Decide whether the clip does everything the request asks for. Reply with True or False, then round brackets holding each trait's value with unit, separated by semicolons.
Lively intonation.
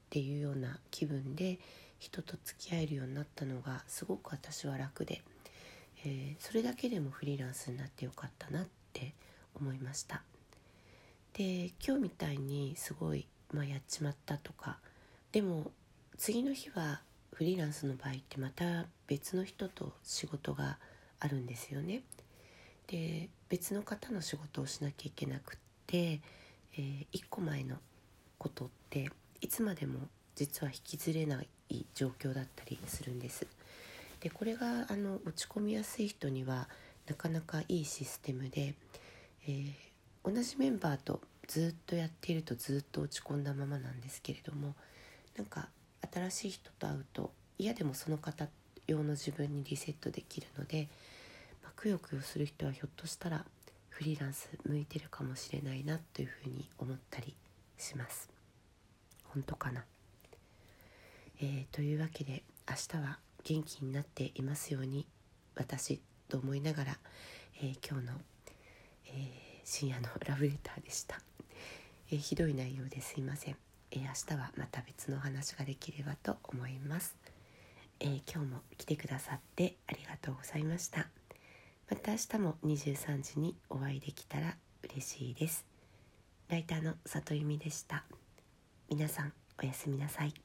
False (3.2 semitones)